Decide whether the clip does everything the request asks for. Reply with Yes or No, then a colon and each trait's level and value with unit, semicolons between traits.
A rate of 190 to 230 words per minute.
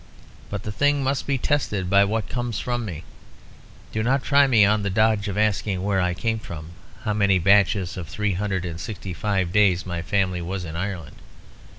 Yes: average, 200 wpm